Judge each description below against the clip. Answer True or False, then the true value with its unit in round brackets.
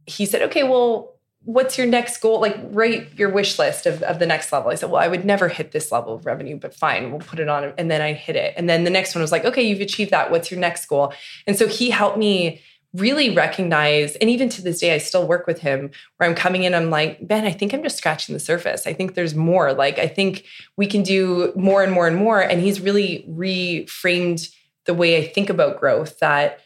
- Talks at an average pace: False (250 wpm)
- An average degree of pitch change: True (4.0 semitones)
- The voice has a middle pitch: True (180 Hz)